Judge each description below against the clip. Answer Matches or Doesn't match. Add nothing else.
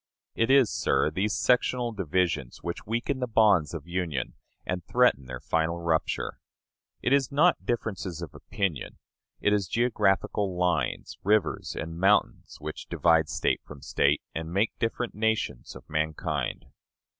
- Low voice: Matches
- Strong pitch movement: Matches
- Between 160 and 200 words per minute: Doesn't match